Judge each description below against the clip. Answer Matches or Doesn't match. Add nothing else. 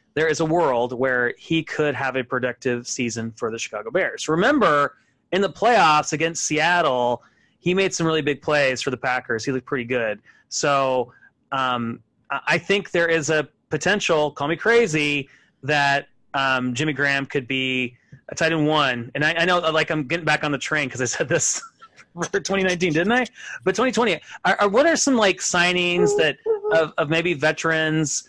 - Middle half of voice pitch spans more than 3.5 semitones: Matches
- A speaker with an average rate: Matches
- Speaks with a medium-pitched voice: Matches